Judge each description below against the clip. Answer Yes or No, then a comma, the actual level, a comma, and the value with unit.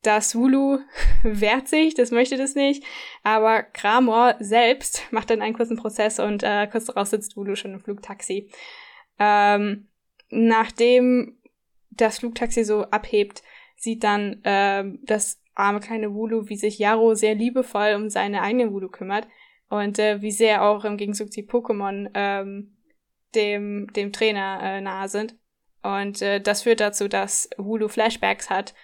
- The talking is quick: No, average, 150 wpm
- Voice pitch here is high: Yes, high, 215 Hz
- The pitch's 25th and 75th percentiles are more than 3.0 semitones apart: No, narrow, 2.4 semitones